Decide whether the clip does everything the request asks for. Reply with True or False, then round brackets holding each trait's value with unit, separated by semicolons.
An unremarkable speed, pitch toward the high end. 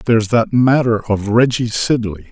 False (155 wpm; 115 Hz)